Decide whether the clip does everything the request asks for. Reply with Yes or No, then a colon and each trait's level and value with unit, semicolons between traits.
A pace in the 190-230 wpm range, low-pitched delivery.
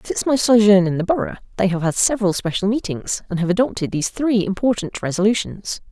No: average, 195 wpm; high, 200 Hz